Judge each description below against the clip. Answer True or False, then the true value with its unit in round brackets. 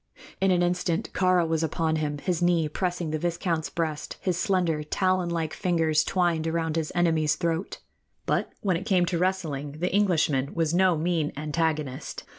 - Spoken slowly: False (170 wpm)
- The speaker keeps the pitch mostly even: True (2.3 semitones)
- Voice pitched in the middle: True (165 Hz)